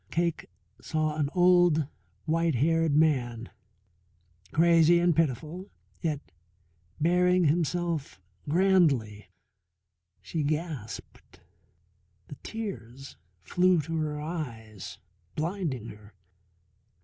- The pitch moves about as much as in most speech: Yes, average, 4.0 semitones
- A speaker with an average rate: No, slow, 85 wpm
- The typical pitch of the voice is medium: Yes, medium, 155 Hz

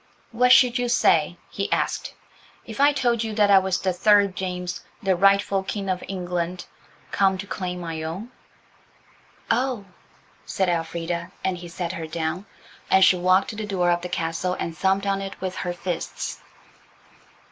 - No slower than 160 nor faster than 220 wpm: Yes, average, 170 wpm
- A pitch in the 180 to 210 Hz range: Yes, high, 190 Hz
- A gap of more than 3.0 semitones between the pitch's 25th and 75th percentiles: No, narrow, 2.4 semitones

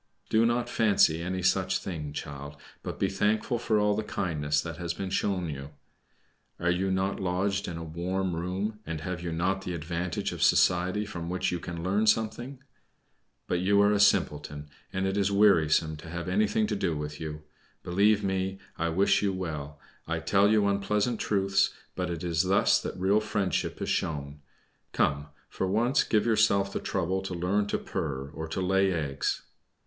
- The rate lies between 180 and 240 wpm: Yes, average, 185 wpm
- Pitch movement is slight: No, average, 3.4 semitones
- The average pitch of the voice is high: No, very low, 95 Hz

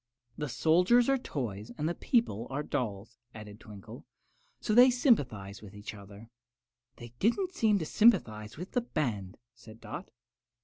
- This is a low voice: Yes, low, 125 Hz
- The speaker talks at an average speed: Yes, average, 150 wpm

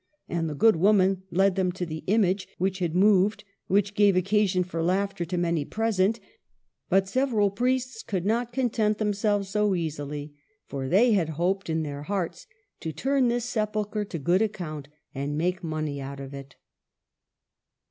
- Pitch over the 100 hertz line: Yes, high, 190 Hz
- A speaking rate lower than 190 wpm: Yes, average, 170 wpm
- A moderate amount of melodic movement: Yes, average, 4.3 semitones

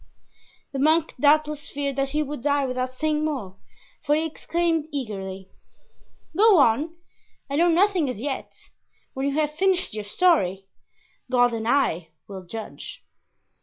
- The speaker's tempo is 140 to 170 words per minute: Yes, average, 145 wpm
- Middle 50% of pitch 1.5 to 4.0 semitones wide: No, average, 4.6 semitones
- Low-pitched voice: No, very high, 285 Hz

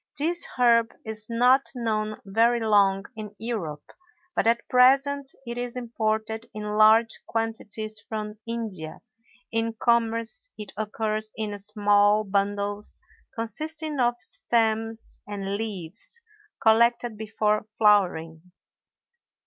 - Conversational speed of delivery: No, slow, 110 wpm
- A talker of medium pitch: No, high, 220 Hz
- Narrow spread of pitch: Yes, narrow, 2.0 semitones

